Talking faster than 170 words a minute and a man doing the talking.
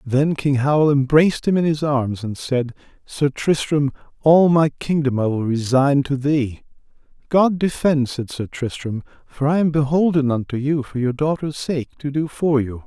Yes: average, 180 wpm; male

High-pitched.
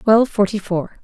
Yes: high, 205 Hz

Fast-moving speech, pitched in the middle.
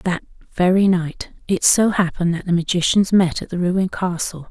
No: average, 185 wpm; medium, 180 Hz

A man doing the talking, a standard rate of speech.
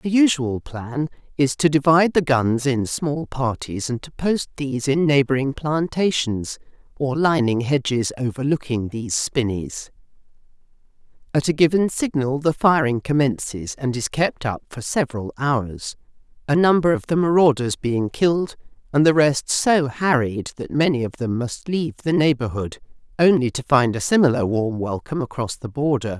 No: female; average, 155 wpm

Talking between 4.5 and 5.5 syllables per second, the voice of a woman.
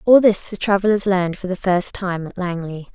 Yes: 5.3 syllables/s; female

